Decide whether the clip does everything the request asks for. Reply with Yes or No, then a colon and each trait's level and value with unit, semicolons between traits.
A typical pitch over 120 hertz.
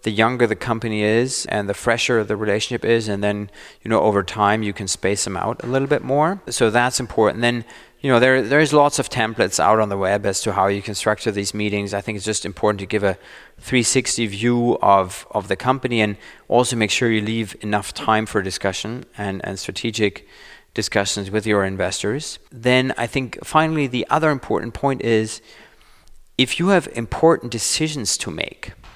No: low, 110 Hz